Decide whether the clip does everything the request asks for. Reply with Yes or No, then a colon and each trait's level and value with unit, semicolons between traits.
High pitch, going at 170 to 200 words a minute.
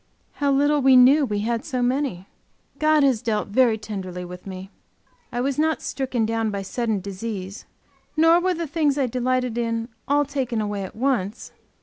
Yes: high, 245 Hz; average, 180 wpm